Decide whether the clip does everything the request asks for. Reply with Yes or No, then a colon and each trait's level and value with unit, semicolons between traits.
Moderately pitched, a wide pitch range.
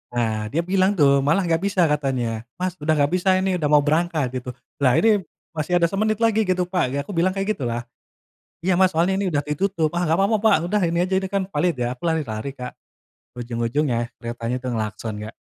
Yes: medium, 160 Hz; wide, 6.7 semitones